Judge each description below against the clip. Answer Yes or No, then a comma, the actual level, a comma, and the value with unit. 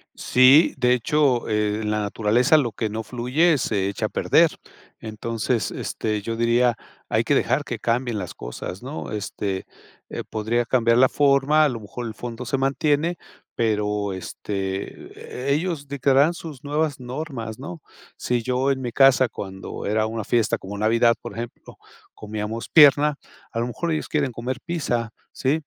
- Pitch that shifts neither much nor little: Yes, average, 4.3 semitones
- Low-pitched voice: Yes, low, 120 Hz